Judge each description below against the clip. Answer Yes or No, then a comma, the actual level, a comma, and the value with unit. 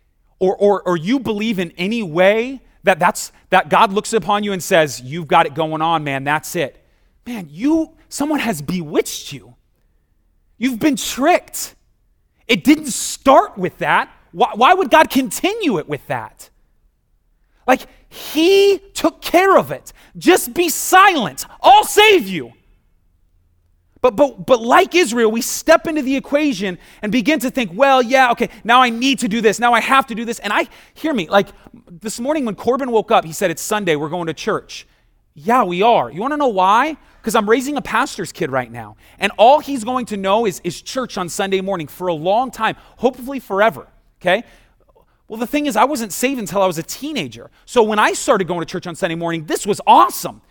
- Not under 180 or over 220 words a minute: Yes, average, 200 wpm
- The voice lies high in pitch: Yes, high, 225 Hz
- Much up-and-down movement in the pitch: Yes, wide, 7.1 semitones